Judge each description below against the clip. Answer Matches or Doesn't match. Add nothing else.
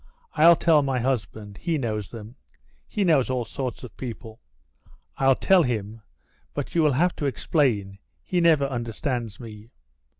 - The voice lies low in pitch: Matches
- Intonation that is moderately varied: Matches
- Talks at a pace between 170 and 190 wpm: Doesn't match